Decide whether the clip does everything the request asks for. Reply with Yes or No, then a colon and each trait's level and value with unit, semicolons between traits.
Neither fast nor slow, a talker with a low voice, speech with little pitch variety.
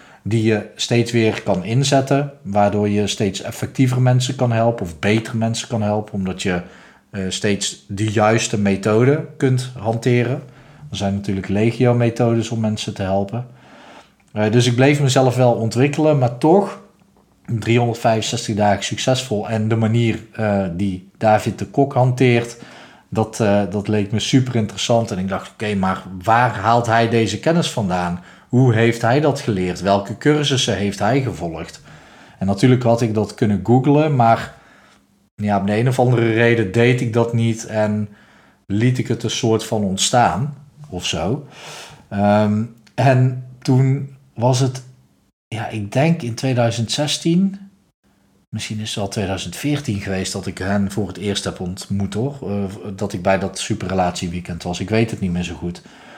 No: average, 165 wpm; low, 115 Hz; average, 3.8 semitones